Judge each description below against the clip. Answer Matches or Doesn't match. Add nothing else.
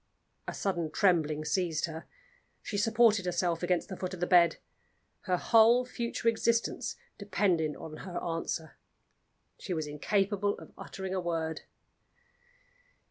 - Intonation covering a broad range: Doesn't match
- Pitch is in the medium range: Matches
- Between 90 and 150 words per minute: Matches